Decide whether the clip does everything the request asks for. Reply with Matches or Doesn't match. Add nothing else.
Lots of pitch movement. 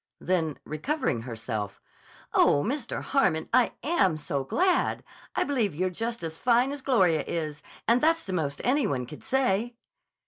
Matches